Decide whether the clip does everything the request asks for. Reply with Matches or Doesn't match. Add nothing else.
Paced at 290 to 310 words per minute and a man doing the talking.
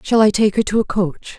Doesn't match